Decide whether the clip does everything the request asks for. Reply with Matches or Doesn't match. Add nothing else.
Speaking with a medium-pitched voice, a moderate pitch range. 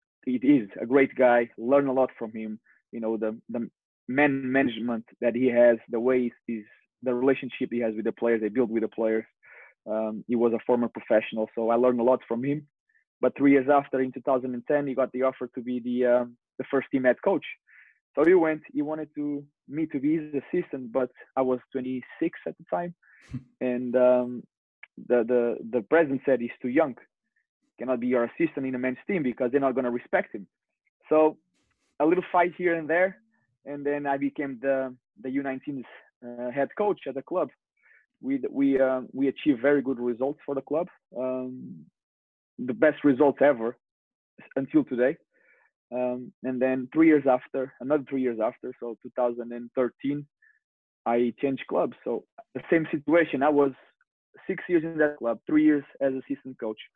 Doesn't match